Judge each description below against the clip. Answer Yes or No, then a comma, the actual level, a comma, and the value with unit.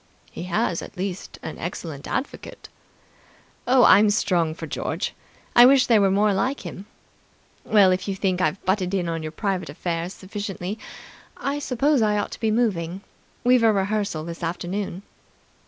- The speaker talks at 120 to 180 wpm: Yes, average, 165 wpm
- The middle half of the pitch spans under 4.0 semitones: Yes, average, 3.4 semitones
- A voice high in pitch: Yes, high, 195 Hz